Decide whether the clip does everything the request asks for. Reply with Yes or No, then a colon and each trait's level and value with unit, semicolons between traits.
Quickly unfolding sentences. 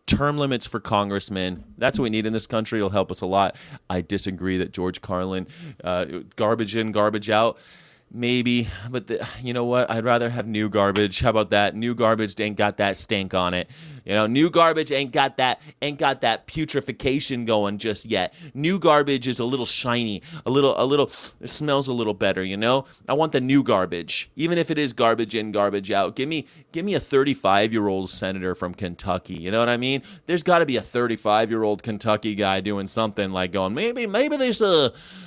Yes: fast, 215 wpm